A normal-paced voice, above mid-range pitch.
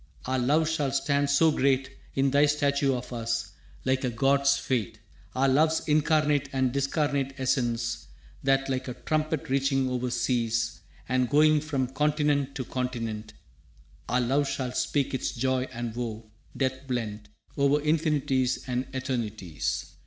No: average, 145 wpm; low, 130 Hz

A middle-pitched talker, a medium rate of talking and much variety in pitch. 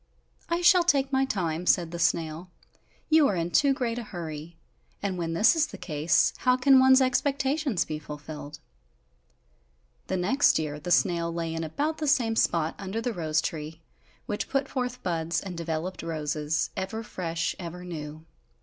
Yes: medium, 175 Hz; average, 170 wpm; wide, 7.8 semitones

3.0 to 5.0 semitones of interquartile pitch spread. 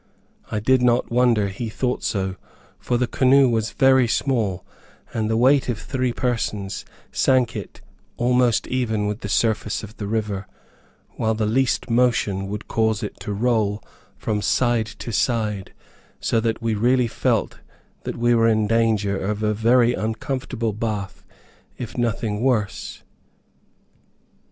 No: narrow, 2.6 semitones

